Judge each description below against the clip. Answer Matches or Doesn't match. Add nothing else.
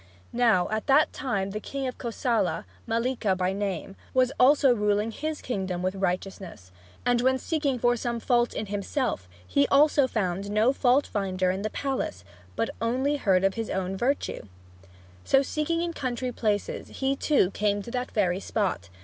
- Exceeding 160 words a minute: Matches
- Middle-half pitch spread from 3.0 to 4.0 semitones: Doesn't match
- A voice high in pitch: Matches